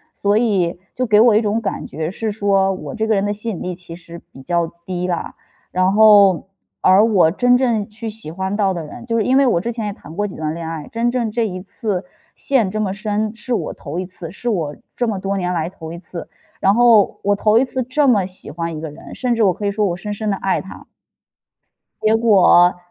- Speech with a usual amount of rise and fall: Yes, average, 3.8 semitones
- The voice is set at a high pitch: Yes, high, 200 Hz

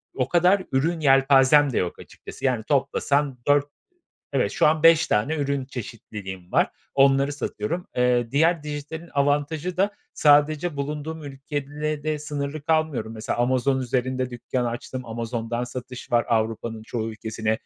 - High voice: No, low, 135 Hz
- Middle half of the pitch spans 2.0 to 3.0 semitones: No, average, 3.7 semitones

